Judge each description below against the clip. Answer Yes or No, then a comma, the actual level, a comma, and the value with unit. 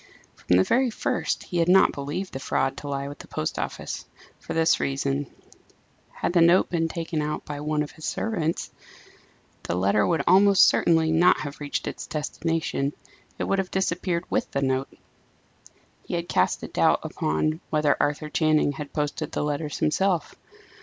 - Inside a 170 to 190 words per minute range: Yes, average, 175 wpm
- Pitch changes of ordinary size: Yes, average, 3.0 semitones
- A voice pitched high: No, medium, 155 Hz